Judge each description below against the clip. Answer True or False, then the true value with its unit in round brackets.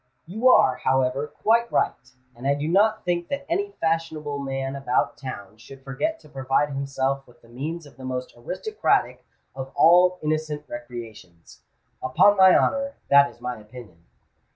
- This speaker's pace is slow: False (160 wpm)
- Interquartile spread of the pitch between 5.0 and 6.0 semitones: True (5.3 semitones)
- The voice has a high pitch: False (140 Hz)